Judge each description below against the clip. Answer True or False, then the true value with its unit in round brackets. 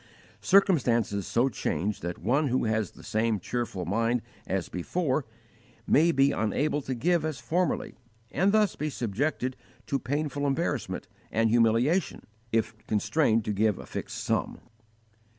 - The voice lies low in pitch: True (125 Hz)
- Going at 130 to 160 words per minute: True (140 wpm)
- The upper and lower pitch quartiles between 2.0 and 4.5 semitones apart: False (5.4 semitones)